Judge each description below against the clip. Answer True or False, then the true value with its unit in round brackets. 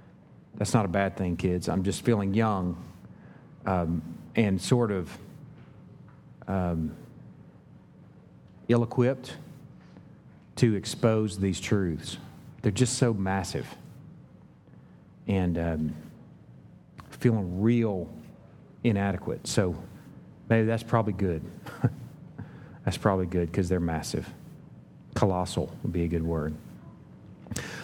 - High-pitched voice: False (100 Hz)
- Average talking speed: False (100 wpm)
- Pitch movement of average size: True (4.9 semitones)